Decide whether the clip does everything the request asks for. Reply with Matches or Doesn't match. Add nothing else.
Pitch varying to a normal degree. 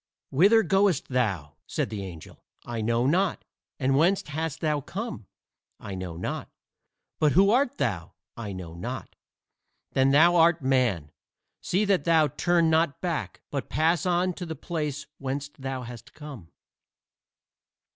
Doesn't match